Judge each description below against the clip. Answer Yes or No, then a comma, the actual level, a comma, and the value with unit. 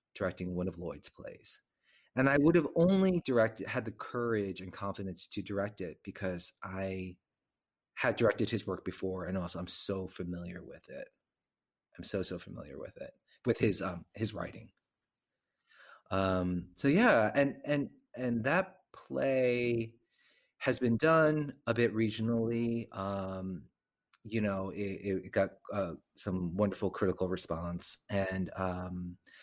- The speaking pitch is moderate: No, low, 100 Hz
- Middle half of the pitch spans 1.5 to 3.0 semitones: No, average, 3.9 semitones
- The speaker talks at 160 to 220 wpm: No, average, 145 wpm